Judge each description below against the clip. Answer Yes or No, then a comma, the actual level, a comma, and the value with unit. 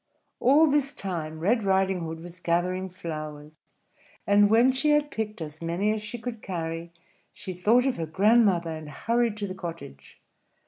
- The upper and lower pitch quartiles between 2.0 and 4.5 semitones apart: No, average, 5.3 semitones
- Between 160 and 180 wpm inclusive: Yes, average, 170 wpm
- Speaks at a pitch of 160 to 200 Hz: Yes, high, 190 Hz